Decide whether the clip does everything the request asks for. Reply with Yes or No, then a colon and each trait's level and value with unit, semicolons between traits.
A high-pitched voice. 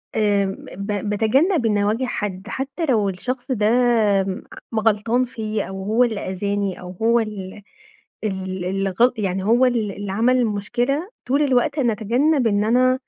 Yes: high, 220 Hz